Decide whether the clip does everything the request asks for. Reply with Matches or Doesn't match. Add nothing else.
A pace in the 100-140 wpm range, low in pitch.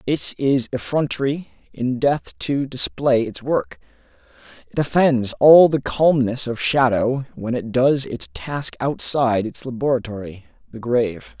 Matches